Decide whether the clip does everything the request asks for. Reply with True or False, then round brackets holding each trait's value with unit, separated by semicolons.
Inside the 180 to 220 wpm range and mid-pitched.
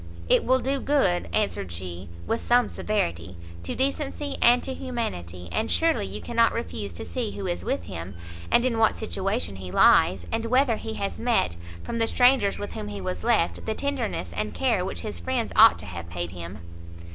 False (195 wpm; 205 Hz)